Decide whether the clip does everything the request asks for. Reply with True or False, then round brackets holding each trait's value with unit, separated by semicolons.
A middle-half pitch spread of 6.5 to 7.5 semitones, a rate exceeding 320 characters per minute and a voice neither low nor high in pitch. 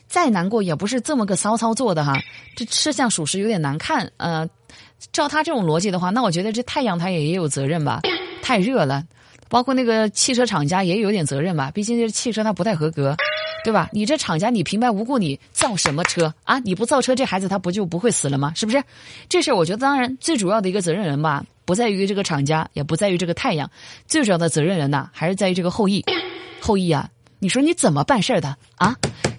False (7.1 semitones; 350 characters per minute; 195 Hz)